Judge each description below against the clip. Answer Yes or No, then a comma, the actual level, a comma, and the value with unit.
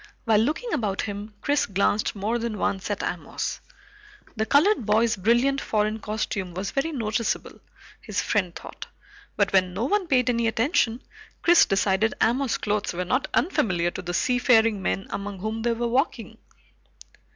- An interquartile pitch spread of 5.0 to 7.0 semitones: No, average, 3.8 semitones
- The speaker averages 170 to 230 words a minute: No, average, 160 wpm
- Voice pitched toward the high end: Yes, high, 220 Hz